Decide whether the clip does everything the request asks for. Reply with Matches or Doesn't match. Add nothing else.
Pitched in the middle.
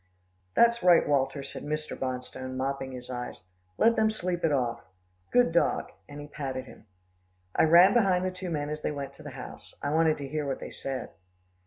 Matches